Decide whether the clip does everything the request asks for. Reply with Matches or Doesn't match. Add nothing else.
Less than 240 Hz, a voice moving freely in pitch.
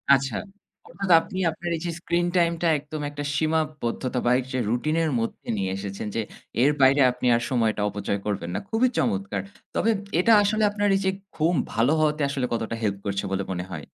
Matches